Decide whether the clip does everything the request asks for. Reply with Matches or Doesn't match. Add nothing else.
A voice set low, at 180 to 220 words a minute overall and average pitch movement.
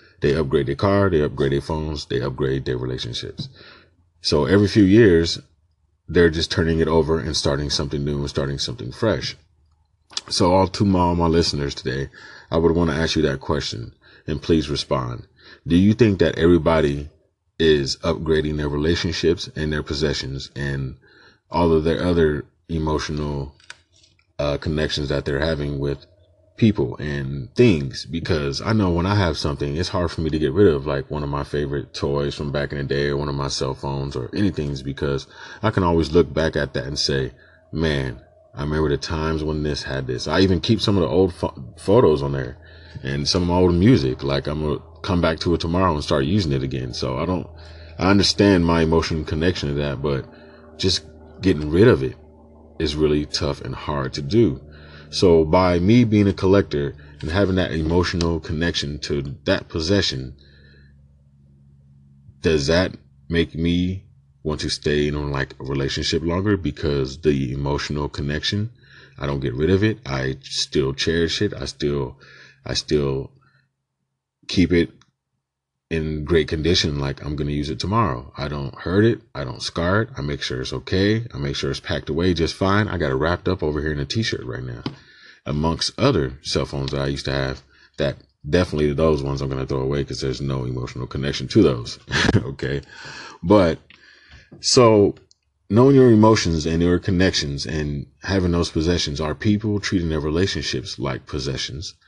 Matches